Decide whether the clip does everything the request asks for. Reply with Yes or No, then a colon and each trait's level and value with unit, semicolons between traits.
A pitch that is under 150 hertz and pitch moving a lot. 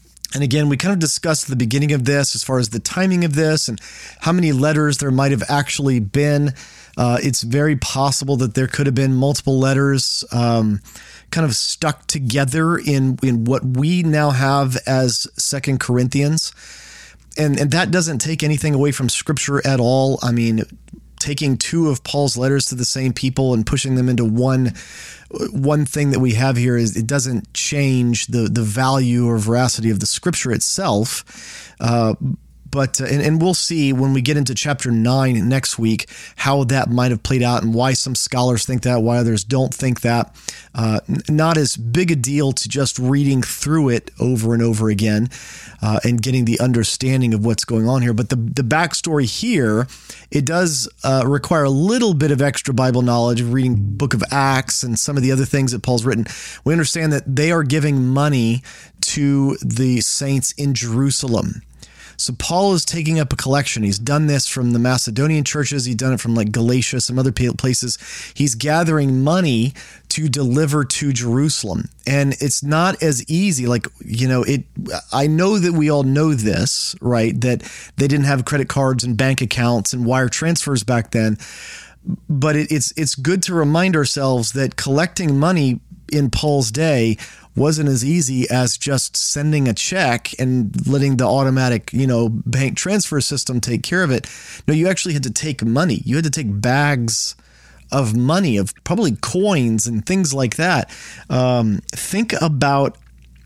No: low, 135 Hz; average, 3.4 semitones